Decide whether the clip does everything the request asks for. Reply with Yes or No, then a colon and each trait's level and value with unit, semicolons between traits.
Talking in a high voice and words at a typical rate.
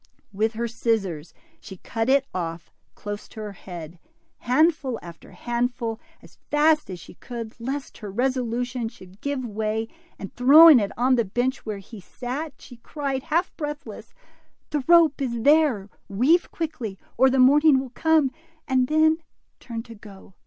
Yes: high, 245 Hz; average, 160 wpm